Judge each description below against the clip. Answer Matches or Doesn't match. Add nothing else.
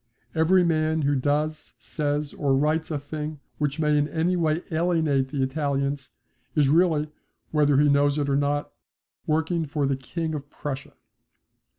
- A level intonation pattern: Matches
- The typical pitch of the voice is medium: Matches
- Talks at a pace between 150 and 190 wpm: Matches